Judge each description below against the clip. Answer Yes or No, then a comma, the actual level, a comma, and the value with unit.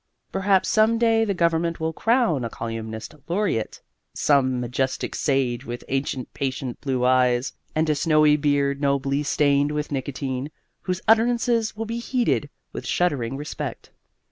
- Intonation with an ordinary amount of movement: No, wide, 5.9 semitones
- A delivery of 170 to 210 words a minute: No, average, 145 wpm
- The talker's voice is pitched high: No, medium, 145 Hz